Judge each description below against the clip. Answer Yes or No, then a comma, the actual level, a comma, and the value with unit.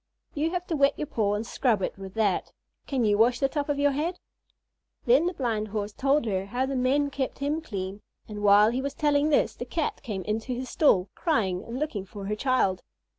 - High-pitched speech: Yes, very high, 250 Hz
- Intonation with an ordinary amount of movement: No, wide, 5.7 semitones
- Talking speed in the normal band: No, fast, 225 wpm